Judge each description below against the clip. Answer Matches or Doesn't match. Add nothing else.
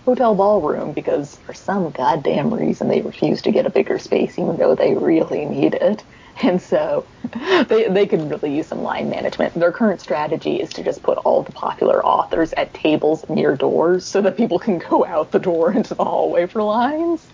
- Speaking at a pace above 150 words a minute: Matches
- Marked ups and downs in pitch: Matches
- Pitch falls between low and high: Doesn't match